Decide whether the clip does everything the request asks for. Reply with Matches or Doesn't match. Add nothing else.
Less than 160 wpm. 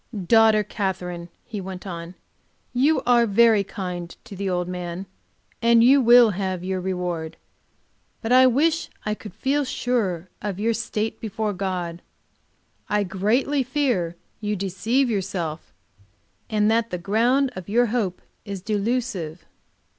Matches